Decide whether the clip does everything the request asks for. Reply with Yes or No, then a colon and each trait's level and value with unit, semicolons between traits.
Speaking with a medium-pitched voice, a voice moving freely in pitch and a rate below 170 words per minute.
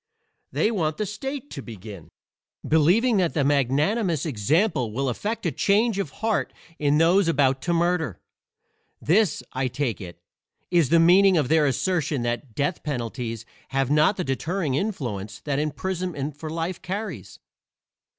Yes: medium, 155 Hz; wide, 5.7 semitones; average, 150 wpm